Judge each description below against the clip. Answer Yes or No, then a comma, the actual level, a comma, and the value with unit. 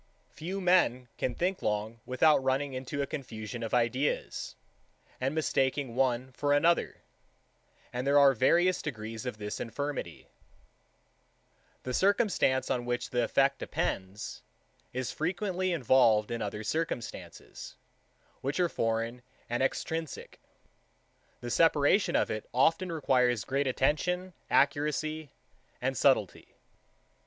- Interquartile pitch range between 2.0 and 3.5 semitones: No, average, 4.6 semitones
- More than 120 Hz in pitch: Yes, low, 135 Hz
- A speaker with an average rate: No, slow, 125 wpm